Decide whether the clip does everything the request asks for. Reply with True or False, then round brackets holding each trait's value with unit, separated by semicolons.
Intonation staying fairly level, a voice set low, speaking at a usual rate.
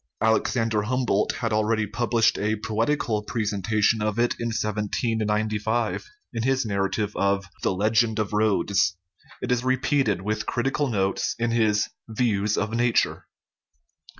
False (2.0 semitones; 110 Hz; 130 wpm)